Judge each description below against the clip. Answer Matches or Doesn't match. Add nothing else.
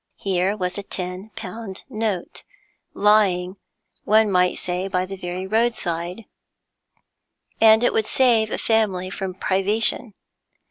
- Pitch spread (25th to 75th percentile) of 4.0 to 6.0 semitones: Doesn't match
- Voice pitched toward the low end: Doesn't match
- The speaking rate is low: Matches